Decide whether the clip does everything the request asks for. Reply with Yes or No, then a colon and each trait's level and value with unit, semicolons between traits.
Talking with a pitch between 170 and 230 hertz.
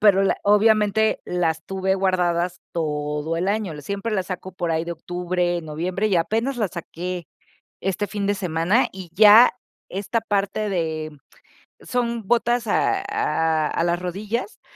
Yes: high, 190 Hz